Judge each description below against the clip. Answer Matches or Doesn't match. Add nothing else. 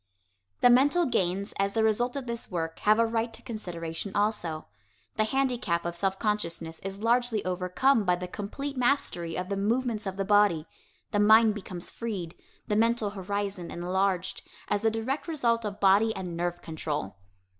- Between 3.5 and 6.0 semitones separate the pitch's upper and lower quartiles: Matches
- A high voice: Matches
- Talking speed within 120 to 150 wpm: Doesn't match